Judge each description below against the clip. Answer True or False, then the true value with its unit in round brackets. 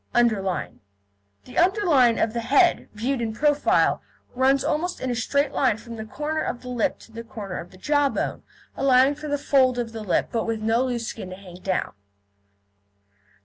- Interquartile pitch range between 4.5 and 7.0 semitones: False (4.1 semitones)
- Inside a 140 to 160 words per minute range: False (190 wpm)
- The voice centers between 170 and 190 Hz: False (245 Hz)